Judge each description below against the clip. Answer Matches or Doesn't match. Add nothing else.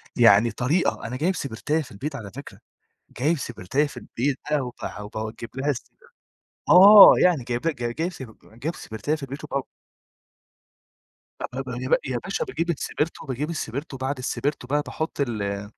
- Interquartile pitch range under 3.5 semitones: Doesn't match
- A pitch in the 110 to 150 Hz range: Matches